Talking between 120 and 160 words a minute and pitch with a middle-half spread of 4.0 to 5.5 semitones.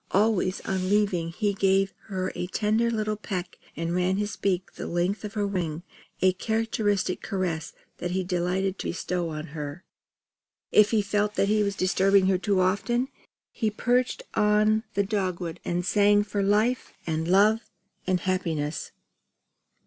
No: average, 155 wpm; narrow, 2.6 semitones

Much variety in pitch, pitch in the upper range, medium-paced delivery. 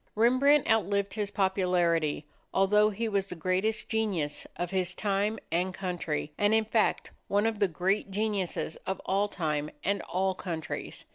No: average, 2.8 semitones; high, 195 Hz; average, 155 wpm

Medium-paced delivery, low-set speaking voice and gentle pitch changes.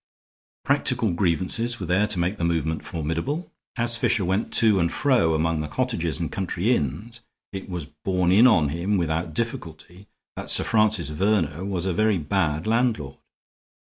No: average, 165 wpm; very low, 95 Hz; average, 5.0 semitones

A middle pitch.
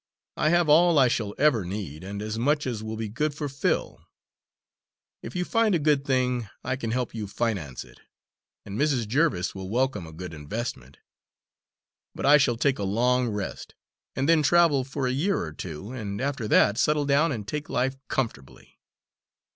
No: low, 125 Hz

